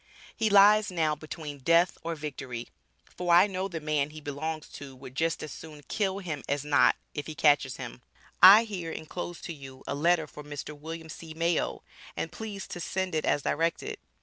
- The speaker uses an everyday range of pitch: Yes, average, 3.4 semitones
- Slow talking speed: No, average, 195 wpm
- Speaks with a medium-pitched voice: Yes, medium, 160 Hz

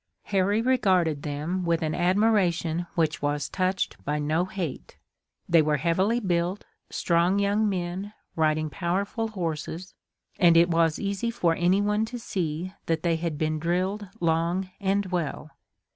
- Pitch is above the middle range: No, medium, 175 Hz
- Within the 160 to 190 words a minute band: No, average, 145 wpm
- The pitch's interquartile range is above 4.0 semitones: No, average, 3.4 semitones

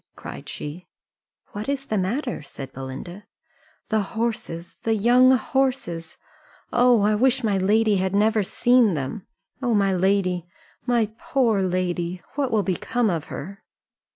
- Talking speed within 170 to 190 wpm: No, average, 140 wpm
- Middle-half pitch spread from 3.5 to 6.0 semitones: Yes, average, 4.8 semitones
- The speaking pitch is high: Yes, high, 210 Hz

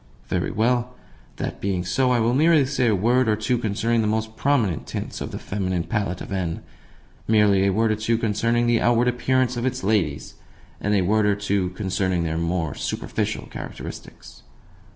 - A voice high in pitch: No, low, 110 Hz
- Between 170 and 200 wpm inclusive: Yes, average, 185 wpm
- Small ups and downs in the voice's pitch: No, average, 3.8 semitones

